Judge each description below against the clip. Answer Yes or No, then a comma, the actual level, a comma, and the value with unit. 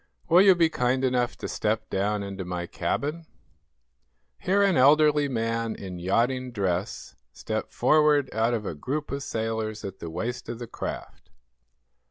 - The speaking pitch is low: Yes, low, 120 Hz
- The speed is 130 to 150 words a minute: No, average, 160 wpm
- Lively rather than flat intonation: Yes, wide, 5.8 semitones